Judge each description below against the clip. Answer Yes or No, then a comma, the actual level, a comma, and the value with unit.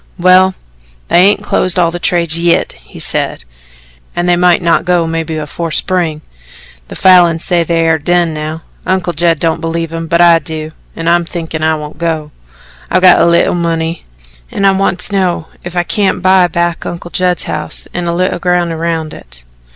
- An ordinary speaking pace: Yes, average, 190 wpm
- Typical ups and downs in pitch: No, narrow, 1.5 semitones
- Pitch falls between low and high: Yes, medium, 170 Hz